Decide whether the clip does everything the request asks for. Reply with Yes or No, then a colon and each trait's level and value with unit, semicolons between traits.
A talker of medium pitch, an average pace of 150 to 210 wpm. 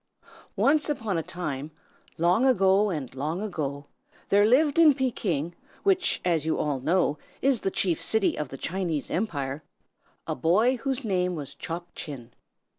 Yes: medium, 180 Hz; average, 155 wpm